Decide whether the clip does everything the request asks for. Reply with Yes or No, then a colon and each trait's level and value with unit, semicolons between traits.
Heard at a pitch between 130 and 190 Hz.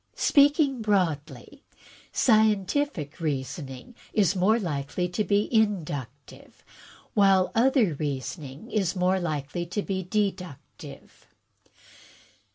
Yes: medium, 185 Hz